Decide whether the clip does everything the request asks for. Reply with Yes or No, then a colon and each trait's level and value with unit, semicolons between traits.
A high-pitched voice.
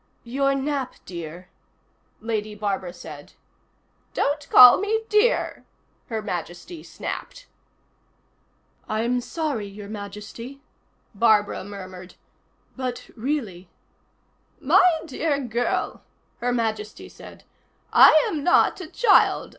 Yes: high, 235 Hz